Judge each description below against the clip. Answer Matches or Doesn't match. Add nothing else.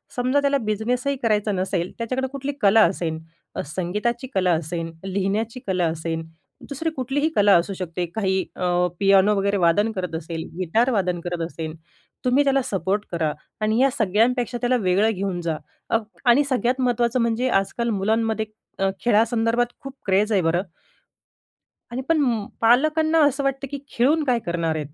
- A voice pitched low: Doesn't match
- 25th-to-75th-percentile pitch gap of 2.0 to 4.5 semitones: Doesn't match